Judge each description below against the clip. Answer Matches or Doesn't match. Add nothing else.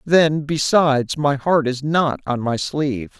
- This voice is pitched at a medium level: Matches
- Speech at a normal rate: Matches